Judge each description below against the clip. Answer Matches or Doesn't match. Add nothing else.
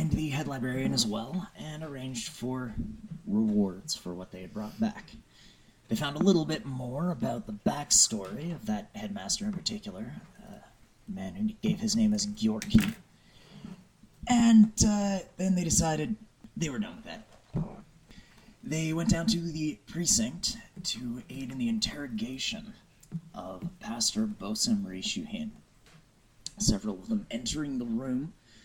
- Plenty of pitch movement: Matches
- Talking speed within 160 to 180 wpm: Doesn't match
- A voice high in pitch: Matches